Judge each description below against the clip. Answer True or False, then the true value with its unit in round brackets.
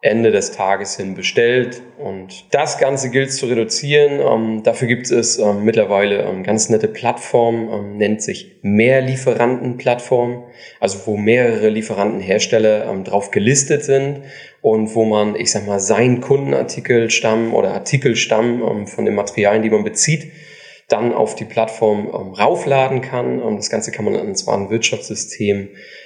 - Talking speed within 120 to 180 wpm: True (155 wpm)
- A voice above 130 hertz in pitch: False (115 Hz)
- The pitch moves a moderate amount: True (3.2 semitones)